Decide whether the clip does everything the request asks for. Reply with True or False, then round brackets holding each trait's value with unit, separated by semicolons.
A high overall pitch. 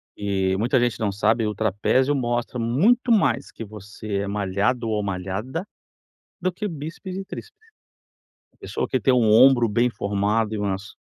False (115 Hz)